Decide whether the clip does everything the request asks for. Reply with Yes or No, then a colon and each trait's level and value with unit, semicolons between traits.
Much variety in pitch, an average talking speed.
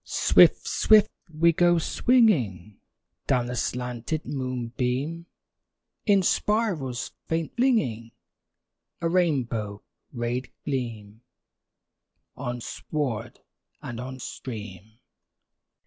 No: wide, 6.1 semitones; slow, 85 wpm